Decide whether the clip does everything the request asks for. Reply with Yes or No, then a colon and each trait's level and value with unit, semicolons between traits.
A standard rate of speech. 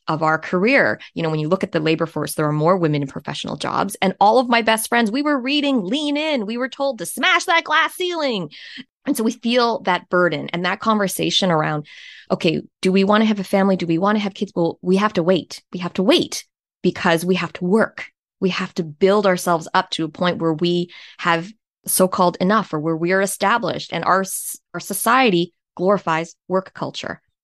No: fast, 225 wpm